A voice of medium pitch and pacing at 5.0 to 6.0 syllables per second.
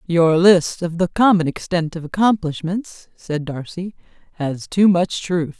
No: medium, 175 Hz; 4.0 syllables/s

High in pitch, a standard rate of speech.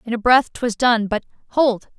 Yes: high, 235 Hz; average, 180 wpm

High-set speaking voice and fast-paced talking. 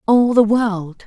No: high, 215 Hz; average, 170 wpm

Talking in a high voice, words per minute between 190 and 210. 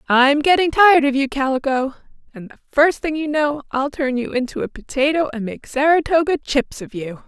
Yes: very high, 280 Hz; average, 200 wpm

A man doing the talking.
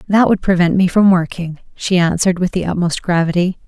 No: female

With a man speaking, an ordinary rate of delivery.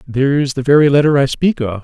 No: male; fast, 260 wpm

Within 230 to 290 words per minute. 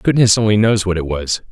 Yes: fast, 240 wpm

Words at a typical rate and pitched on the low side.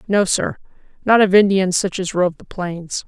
No: average, 195 wpm; medium, 185 Hz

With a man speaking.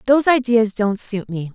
No: female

